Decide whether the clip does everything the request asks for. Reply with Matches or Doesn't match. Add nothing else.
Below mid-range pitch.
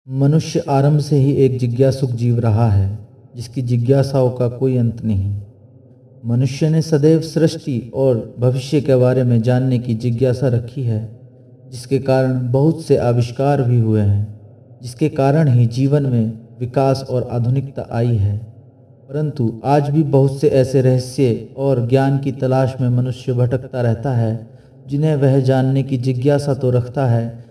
Matches